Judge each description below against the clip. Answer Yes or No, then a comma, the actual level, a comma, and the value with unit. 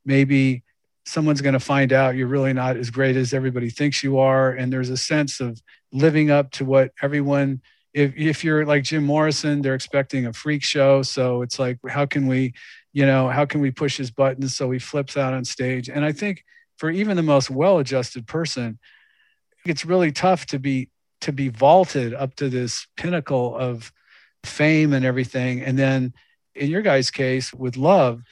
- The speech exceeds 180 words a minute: Yes, average, 190 wpm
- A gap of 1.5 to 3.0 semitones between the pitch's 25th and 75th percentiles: Yes, narrow, 2.4 semitones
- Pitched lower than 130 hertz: No, low, 135 Hz